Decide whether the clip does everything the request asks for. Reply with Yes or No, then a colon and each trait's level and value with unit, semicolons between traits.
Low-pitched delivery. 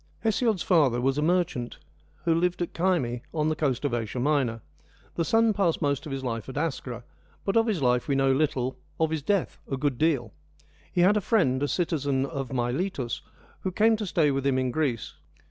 No: medium, 145 Hz